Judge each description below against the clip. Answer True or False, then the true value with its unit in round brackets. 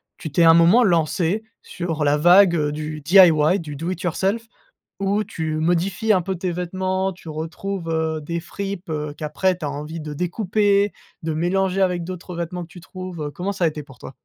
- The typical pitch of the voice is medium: True (175 Hz)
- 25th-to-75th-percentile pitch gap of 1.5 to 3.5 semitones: True (3.2 semitones)